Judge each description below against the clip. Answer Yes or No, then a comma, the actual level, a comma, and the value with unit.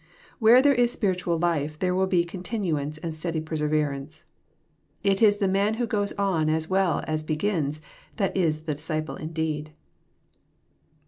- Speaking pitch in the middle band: Yes, medium, 170 Hz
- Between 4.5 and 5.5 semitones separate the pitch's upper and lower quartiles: No, average, 4.1 semitones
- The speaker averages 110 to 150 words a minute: No, average, 165 wpm